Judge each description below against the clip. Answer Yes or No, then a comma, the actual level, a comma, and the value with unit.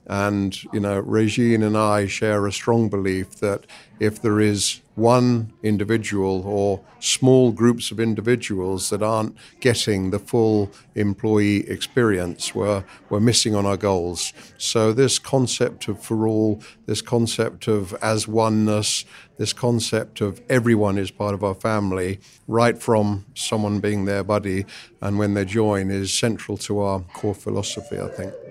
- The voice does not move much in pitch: Yes, narrow, 2.1 semitones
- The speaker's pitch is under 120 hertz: Yes, low, 105 Hz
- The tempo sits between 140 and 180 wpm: Yes, average, 150 wpm